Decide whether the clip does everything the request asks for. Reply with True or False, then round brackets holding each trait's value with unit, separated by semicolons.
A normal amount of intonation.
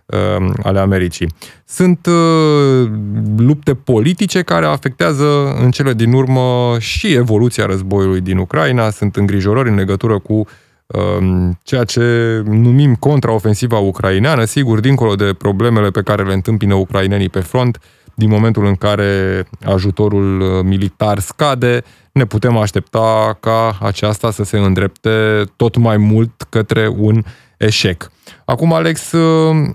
True (3.8 semitones)